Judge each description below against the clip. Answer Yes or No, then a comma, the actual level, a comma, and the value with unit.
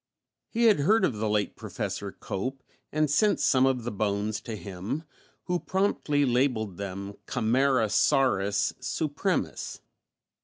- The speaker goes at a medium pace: No, slow, 125 wpm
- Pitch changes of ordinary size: No, wide, 5.8 semitones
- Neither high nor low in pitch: No, low, 125 Hz